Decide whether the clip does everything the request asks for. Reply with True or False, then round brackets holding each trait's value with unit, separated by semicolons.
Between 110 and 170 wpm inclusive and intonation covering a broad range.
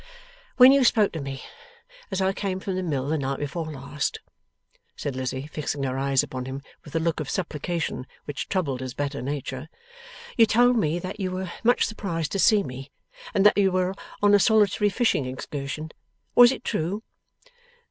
False (185 wpm; 6.2 semitones)